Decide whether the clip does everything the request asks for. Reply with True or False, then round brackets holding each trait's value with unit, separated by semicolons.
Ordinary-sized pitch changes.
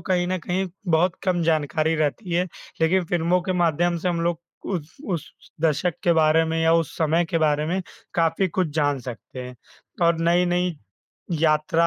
False (1.9 semitones)